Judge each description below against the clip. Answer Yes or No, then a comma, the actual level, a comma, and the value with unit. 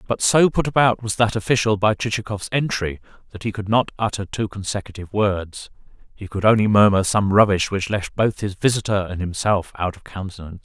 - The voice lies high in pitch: No, low, 105 Hz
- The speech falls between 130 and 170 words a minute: No, average, 185 wpm